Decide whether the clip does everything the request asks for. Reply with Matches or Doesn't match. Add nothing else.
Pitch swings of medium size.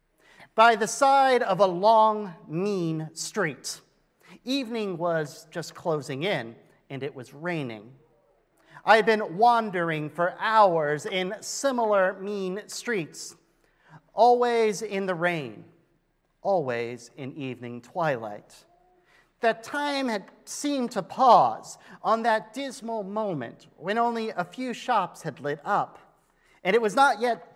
Doesn't match